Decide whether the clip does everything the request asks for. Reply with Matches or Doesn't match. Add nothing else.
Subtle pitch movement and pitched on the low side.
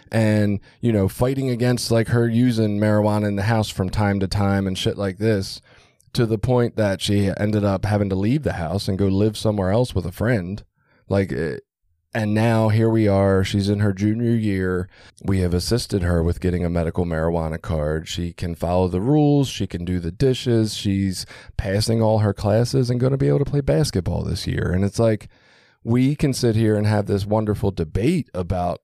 Doesn't match